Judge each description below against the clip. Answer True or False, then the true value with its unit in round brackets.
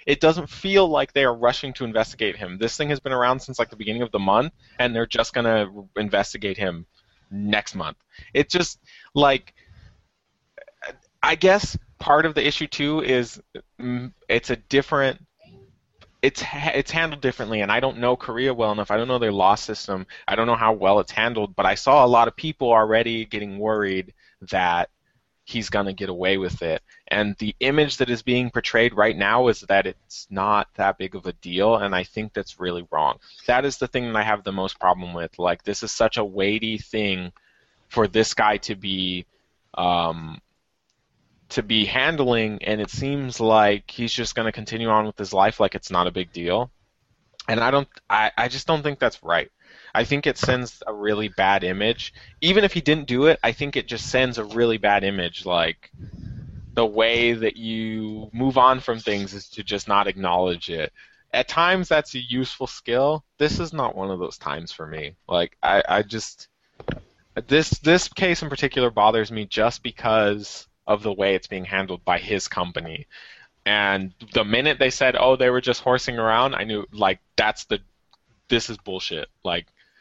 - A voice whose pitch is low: True (115 Hz)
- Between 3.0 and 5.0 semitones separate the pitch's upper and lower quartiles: True (4.1 semitones)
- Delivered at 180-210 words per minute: True (195 wpm)